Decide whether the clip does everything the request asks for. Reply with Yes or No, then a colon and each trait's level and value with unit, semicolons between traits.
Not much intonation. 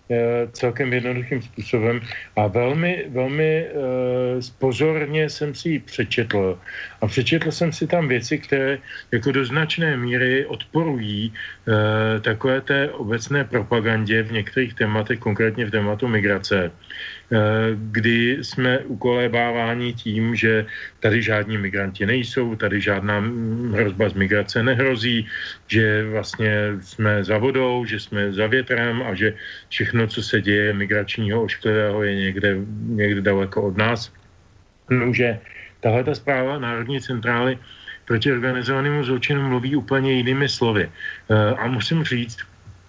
No: average, 3.2 semitones